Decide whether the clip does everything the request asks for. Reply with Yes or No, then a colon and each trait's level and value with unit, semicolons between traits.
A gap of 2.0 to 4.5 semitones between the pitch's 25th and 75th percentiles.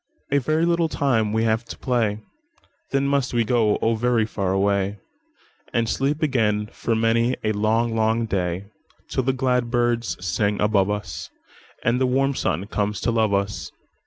Yes: average, 3.5 semitones